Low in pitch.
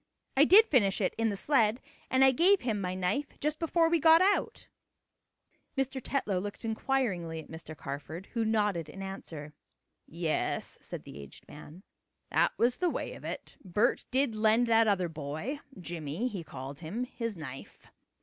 No: high, 210 Hz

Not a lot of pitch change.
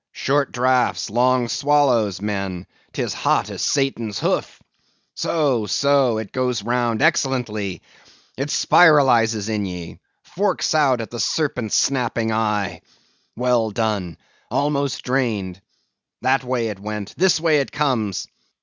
No: average, 4.4 semitones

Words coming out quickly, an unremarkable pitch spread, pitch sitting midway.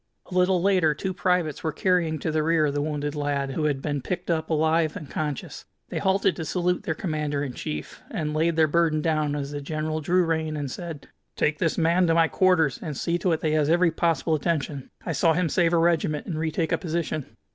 No: fast, 230 wpm; narrow, 2.2 semitones; medium, 160 Hz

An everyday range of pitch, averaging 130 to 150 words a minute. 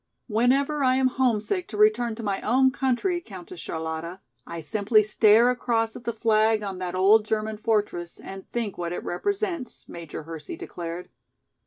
No: average, 5.0 semitones; average, 165 wpm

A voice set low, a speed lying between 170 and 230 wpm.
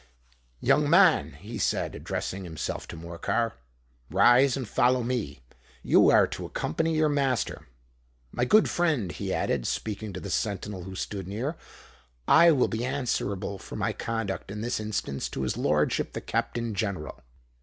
No: low, 110 Hz; average, 155 wpm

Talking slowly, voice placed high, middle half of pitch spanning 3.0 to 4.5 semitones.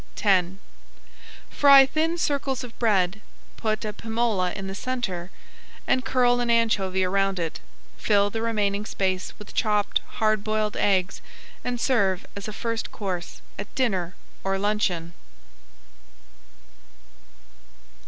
Yes: slow, 125 wpm; high, 210 Hz; average, 3.4 semitones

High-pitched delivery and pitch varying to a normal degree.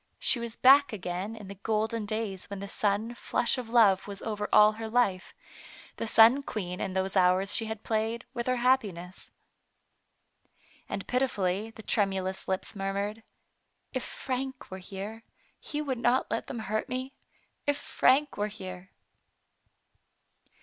Yes: high, 215 Hz; average, 3.6 semitones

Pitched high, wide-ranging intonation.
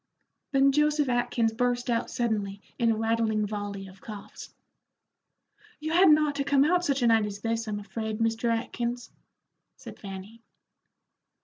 No: high, 230 Hz; average, 4.0 semitones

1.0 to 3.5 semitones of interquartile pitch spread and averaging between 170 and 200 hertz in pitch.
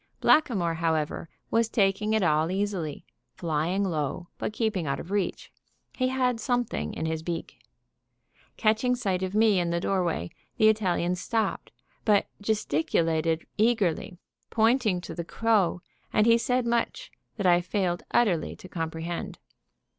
No: average, 4.7 semitones; high, 190 Hz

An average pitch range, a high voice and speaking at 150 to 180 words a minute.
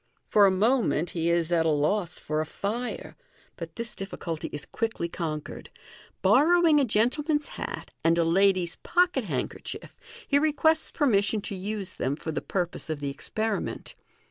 No: wide, 6.5 semitones; high, 195 Hz; average, 165 wpm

